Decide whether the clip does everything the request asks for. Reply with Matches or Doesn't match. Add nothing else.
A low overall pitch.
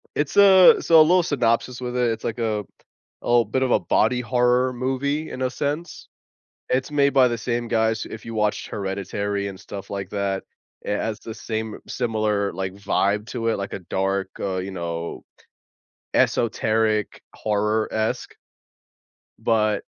Matches